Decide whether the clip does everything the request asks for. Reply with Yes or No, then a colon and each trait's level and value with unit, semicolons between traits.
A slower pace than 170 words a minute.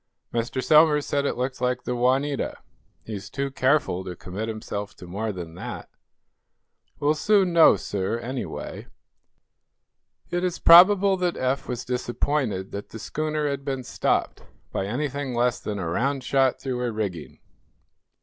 Yes: average, 155 wpm